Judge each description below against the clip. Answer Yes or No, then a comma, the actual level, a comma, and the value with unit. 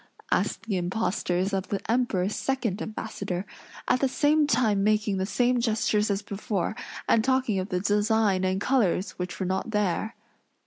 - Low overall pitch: No, high, 210 Hz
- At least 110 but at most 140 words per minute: No, average, 165 wpm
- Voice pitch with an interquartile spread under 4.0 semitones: Yes, average, 3.3 semitones